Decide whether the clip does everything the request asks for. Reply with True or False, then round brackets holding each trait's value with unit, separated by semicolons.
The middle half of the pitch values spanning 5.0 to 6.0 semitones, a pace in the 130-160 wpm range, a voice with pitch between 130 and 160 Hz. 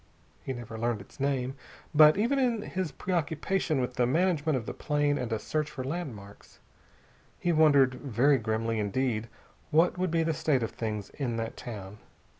False (5.6 semitones; 175 wpm; 135 Hz)